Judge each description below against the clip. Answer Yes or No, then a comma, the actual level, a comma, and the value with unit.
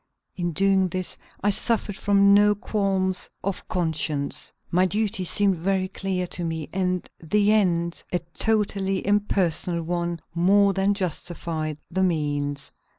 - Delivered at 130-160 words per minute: Yes, slow, 135 wpm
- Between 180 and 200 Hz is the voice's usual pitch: Yes, medium, 185 Hz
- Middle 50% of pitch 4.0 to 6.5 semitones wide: No, average, 2.7 semitones